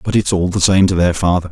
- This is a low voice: Yes, very low, 90 Hz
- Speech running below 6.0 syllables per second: No, 6.4 syllables/s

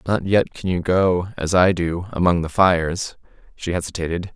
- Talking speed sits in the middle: Yes, average, 165 wpm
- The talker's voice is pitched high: No, very low, 90 Hz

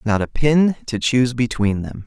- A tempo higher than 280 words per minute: No, fast, 205 wpm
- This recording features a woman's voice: No, male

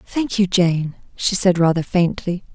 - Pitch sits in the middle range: Yes, medium, 180 Hz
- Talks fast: No, average, 165 wpm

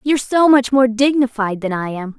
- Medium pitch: No, high, 245 Hz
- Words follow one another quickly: Yes, fast, 220 wpm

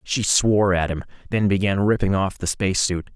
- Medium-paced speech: Yes, average, 190 wpm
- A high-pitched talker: No, low, 100 Hz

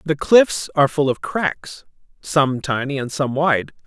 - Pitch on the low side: No, medium, 145 Hz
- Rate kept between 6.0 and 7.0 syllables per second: No, 4.0 syllables/s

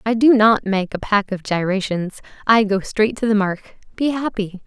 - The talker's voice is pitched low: No, high, 210 Hz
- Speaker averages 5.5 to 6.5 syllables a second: No, 4.6 syllables/s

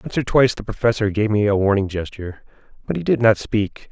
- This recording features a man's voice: Yes, male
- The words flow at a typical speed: No, fast, 230 wpm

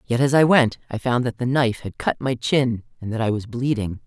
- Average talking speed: No, fast, 265 wpm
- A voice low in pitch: Yes, low, 120 Hz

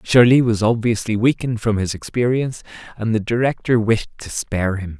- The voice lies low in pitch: Yes, low, 115 Hz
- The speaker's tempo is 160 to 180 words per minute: Yes, average, 170 wpm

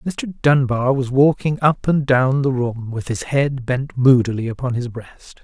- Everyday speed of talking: Yes, average, 190 wpm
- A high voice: No, low, 130 Hz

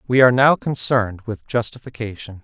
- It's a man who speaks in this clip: Yes, male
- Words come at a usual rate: Yes, average, 150 wpm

